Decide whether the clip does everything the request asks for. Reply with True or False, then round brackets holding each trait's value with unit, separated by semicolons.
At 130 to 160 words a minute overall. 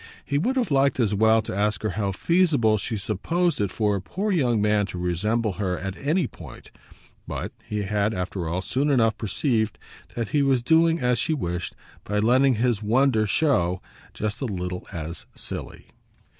False (185 wpm)